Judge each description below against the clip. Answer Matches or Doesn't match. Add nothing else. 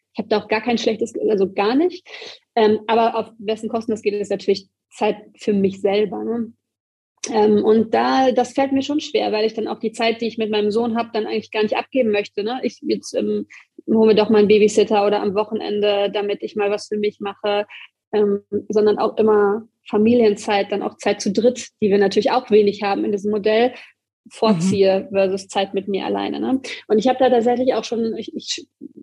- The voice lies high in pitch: Matches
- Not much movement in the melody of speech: Matches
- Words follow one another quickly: Matches